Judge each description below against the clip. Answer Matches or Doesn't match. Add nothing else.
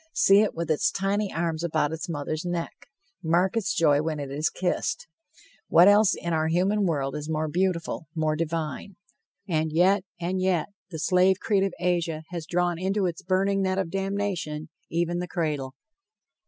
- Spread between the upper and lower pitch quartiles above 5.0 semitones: Doesn't match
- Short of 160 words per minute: Doesn't match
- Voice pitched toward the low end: Doesn't match